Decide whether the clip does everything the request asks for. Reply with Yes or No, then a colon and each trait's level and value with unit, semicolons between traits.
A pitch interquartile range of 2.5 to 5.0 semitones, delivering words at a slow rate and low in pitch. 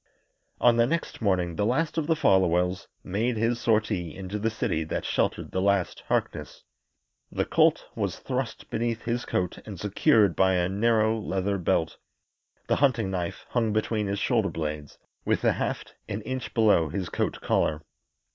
No: average, 4.1 semitones; average, 165 wpm; low, 105 Hz